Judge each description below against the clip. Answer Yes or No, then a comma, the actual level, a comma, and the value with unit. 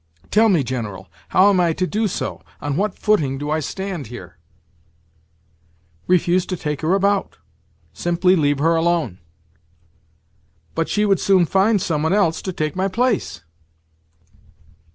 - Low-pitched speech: No, medium, 175 Hz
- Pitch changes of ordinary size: Yes, average, 4.6 semitones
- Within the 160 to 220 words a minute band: No, average, 150 wpm